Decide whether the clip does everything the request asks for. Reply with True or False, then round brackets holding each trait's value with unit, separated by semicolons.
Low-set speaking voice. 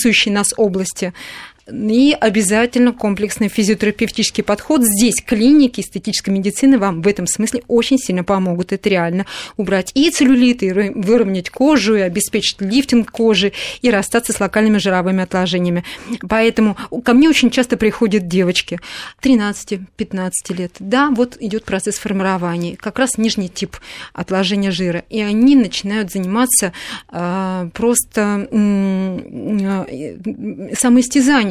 False (210 Hz)